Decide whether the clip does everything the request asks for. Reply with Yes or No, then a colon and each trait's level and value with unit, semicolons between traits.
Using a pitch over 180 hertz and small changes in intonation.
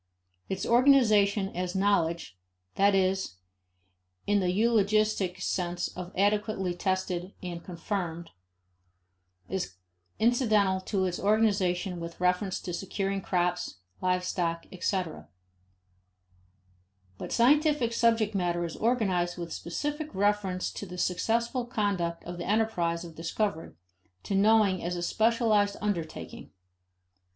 No: high, 190 Hz; average, 3.3 semitones